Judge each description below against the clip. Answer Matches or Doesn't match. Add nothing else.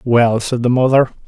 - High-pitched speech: Doesn't match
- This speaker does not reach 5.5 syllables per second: Matches